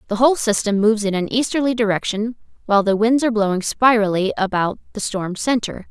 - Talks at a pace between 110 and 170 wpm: No, average, 185 wpm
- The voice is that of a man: No, female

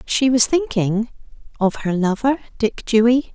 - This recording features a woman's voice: Yes, female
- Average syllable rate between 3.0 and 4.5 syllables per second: Yes, 4.3 syllables/s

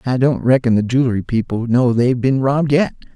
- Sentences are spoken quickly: Yes, fast, 210 wpm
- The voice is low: Yes, low, 125 Hz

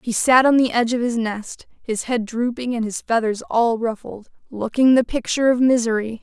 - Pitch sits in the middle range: No, high, 235 Hz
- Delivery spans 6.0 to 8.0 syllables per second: No, 5.2 syllables/s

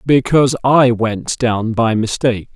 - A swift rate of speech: No, average, 140 wpm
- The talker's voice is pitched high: No, low, 120 Hz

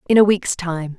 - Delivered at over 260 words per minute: No, fast, 245 wpm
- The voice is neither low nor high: Yes, medium, 180 Hz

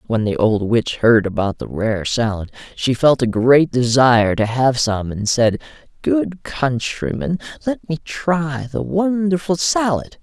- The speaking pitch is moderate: No, low, 130 Hz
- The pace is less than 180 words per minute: Yes, average, 160 wpm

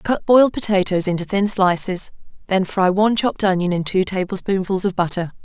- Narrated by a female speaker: Yes, female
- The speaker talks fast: No, average, 175 wpm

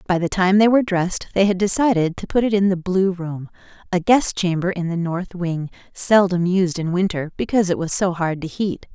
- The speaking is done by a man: No, female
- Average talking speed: No, fast, 230 wpm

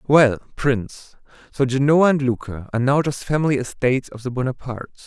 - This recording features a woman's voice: No, male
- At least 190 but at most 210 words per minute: No, average, 165 wpm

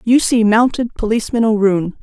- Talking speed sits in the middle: Yes, average, 150 wpm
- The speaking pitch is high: Yes, high, 220 Hz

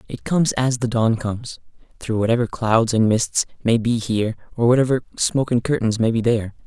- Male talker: Yes, male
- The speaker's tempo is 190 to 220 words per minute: Yes, average, 200 wpm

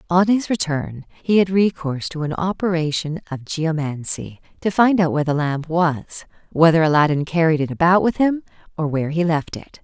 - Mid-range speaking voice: Yes, medium, 165 Hz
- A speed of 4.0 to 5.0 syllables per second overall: No, 5.4 syllables/s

